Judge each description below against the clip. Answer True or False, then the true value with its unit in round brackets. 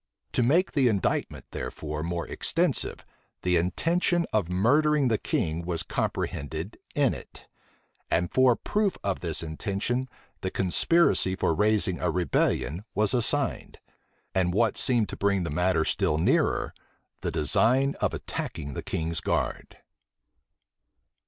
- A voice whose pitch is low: True (100 Hz)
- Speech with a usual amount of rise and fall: False (7.1 semitones)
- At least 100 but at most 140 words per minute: True (135 wpm)